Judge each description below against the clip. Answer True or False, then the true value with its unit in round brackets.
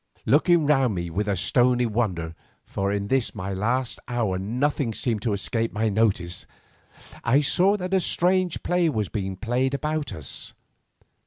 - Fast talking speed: False (160 wpm)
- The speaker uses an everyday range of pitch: False (6.2 semitones)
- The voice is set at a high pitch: False (115 Hz)